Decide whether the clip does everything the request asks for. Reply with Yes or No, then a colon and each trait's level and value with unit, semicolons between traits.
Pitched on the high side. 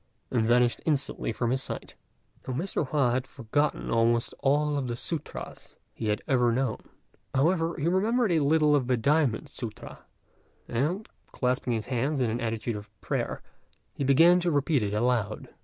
No: low, 130 Hz